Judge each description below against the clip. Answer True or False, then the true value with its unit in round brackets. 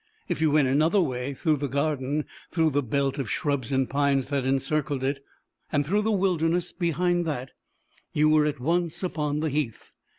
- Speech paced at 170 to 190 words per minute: True (185 wpm)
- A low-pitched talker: False (145 Hz)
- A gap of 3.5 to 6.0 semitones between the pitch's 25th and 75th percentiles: False (3.0 semitones)